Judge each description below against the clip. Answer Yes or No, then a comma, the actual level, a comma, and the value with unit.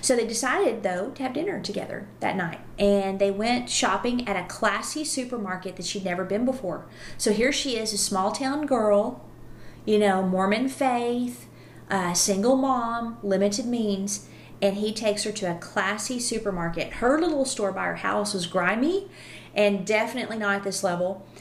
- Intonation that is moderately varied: Yes, average, 3.9 semitones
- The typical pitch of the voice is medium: No, high, 210 Hz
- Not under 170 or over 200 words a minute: Yes, average, 175 wpm